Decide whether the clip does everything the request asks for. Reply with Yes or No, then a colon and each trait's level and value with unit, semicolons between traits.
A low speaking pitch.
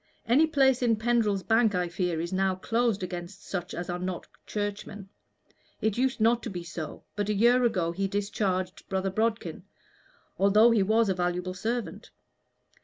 No: high, 200 Hz